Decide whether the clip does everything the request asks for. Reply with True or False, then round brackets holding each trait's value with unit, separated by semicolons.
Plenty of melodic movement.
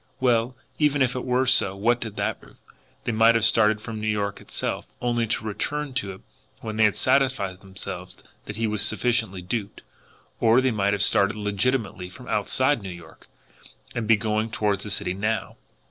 False (3.1 semitones)